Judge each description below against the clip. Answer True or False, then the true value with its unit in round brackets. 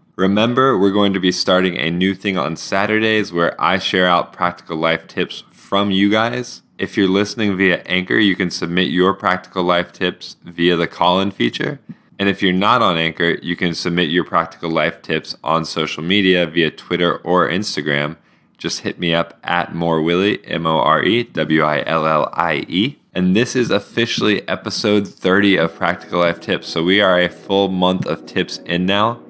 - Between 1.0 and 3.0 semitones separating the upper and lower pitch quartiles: True (2.6 semitones)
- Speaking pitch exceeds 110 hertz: False (90 Hz)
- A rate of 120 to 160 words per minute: False (170 wpm)